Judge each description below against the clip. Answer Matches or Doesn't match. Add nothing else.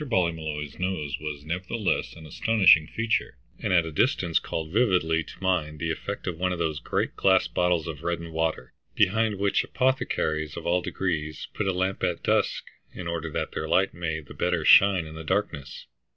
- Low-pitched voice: Matches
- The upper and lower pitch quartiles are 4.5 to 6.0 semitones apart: Doesn't match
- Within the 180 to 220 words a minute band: Matches